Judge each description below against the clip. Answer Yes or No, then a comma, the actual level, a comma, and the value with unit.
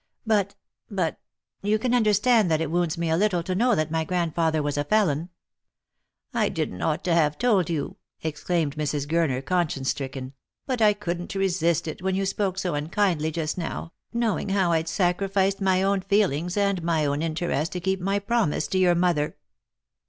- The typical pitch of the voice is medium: Yes, medium, 175 Hz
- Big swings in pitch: No, average, 3.7 semitones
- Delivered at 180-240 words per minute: Yes, average, 195 wpm